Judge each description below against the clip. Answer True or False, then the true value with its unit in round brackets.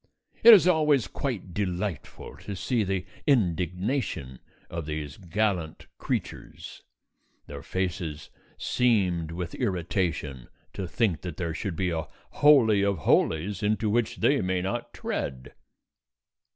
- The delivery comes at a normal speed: False (125 wpm)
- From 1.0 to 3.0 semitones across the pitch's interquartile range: False (4.6 semitones)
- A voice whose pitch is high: False (95 Hz)